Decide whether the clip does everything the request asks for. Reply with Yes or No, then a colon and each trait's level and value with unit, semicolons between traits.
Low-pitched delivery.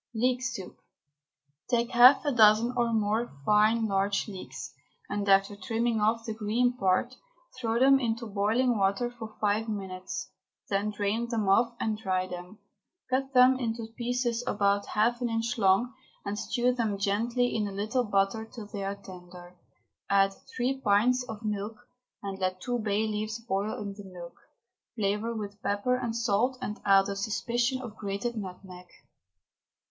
No: high, 215 Hz